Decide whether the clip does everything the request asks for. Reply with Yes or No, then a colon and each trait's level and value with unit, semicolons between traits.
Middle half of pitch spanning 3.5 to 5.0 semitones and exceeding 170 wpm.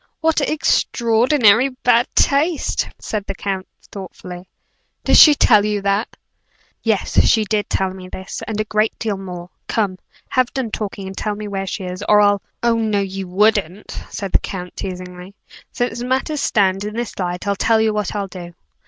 No: average, 3.1 semitones; average, 180 wpm